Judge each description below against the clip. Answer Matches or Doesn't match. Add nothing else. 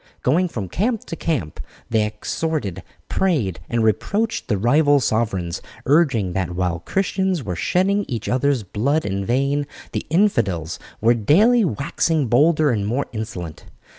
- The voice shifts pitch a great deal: Matches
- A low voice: Matches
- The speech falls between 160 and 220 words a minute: Doesn't match